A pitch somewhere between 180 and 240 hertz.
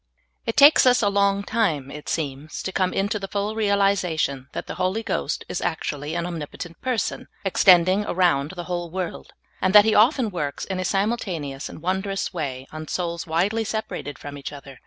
Yes: medium, 185 Hz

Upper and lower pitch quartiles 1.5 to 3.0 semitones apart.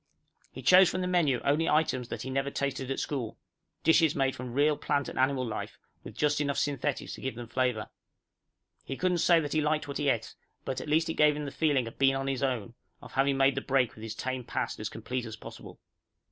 Yes: average, 2.7 semitones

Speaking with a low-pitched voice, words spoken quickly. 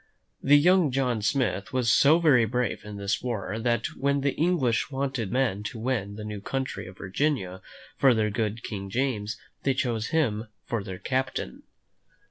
No: low, 120 Hz; average, 170 wpm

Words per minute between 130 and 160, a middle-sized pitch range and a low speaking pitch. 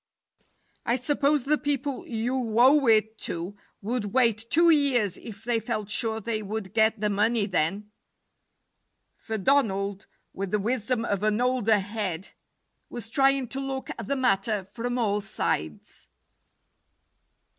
No: average, 140 wpm; average, 3.7 semitones; high, 225 Hz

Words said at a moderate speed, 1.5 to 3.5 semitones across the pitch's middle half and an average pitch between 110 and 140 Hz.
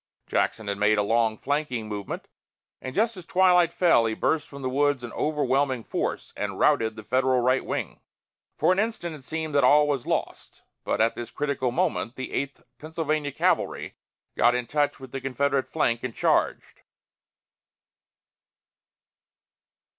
No: average, 160 wpm; average, 4.2 semitones; low, 135 Hz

